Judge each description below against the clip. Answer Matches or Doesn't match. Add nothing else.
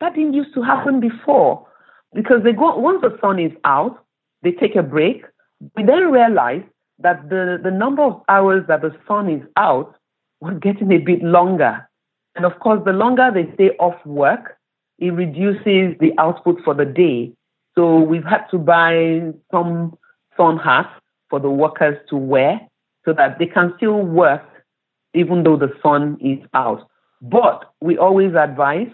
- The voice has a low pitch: Doesn't match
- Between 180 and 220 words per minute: Doesn't match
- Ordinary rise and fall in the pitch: Matches